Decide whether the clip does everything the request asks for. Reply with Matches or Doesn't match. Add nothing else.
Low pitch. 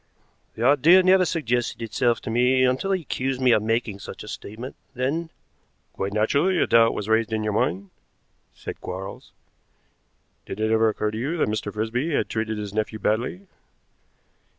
Matches